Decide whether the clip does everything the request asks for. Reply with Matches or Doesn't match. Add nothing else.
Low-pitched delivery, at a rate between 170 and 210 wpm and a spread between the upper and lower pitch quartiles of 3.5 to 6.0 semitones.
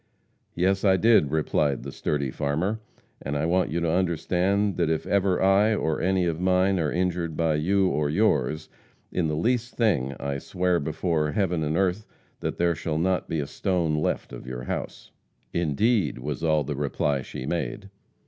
Matches